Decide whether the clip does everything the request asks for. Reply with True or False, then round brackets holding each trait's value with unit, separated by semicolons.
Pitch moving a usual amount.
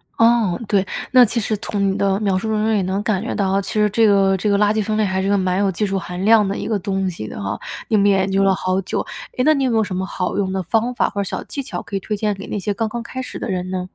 False (2.3 semitones)